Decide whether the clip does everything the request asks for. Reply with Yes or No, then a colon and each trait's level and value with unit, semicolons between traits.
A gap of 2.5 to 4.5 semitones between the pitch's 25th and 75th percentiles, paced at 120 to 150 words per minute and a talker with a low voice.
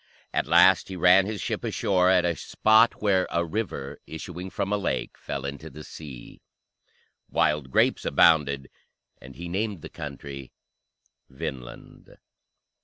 No: average, 5.1 semitones; average, 140 wpm; very low, 85 Hz